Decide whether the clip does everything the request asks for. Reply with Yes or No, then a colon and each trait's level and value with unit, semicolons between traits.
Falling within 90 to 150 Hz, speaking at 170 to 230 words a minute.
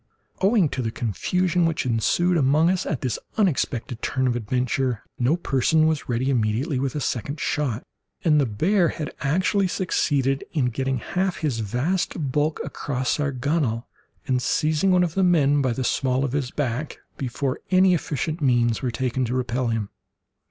Yes: low, 135 Hz; average, 175 wpm